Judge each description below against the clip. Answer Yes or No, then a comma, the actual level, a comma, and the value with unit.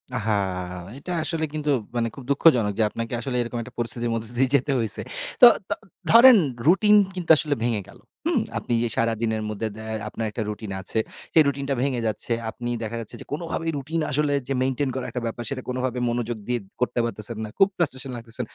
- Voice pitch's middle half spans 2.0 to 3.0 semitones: No, average, 3.9 semitones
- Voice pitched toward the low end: Yes, low, 125 Hz